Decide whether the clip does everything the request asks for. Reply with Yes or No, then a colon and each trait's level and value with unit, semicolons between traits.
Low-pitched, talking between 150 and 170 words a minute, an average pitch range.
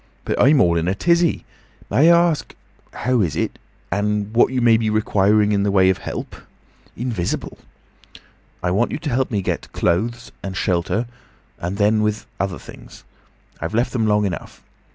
Yes: low, 105 Hz; average, 160 wpm; average, 3.9 semitones